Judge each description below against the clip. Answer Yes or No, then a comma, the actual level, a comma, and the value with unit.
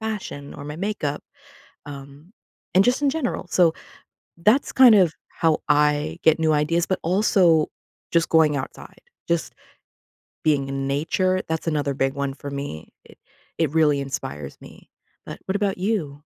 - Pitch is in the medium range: Yes, medium, 160 Hz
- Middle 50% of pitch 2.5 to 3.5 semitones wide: No, average, 4.7 semitones